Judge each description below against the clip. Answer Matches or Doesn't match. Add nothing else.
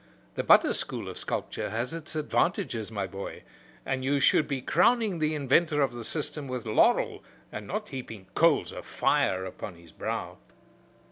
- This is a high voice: Doesn't match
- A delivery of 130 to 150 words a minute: Doesn't match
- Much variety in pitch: Matches